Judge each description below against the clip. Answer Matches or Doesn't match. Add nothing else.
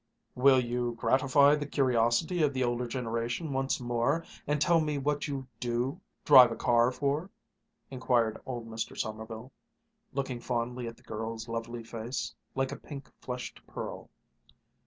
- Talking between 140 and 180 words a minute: Matches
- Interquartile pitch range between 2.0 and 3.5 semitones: Matches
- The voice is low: Matches